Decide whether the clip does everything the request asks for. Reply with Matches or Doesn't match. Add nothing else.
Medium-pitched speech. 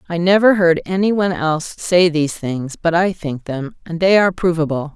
Matches